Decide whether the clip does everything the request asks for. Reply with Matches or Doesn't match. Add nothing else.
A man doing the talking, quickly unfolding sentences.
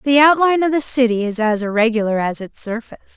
Doesn't match